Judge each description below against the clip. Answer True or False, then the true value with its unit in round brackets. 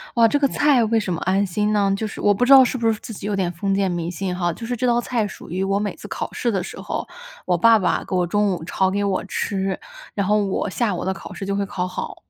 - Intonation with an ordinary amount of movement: True (3.2 semitones)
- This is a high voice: True (200 Hz)